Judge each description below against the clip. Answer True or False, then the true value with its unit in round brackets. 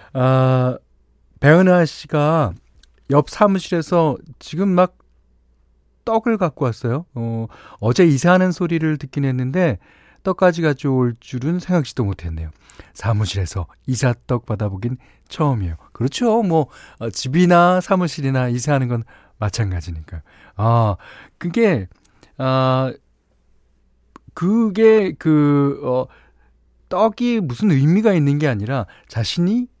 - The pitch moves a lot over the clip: True (8.3 semitones)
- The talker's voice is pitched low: True (130 Hz)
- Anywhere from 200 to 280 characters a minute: True (235 characters per minute)